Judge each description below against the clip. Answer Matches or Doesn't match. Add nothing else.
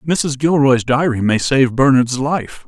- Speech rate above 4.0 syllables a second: Doesn't match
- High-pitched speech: Doesn't match